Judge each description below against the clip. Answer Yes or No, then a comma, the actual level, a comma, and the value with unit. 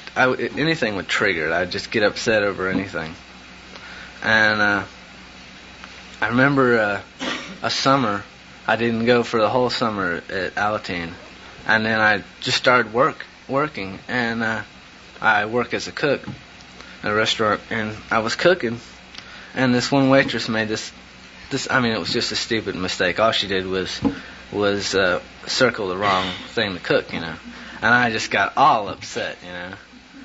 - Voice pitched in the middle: No, low, 105 Hz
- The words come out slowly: No, average, 170 wpm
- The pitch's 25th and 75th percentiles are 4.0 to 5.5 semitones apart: Yes, average, 4.5 semitones